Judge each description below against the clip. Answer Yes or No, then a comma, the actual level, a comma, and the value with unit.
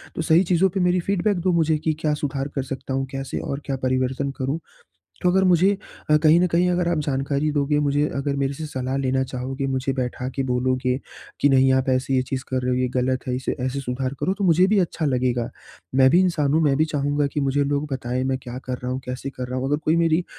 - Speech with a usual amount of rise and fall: Yes, average, 3.4 semitones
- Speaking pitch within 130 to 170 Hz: Yes, medium, 140 Hz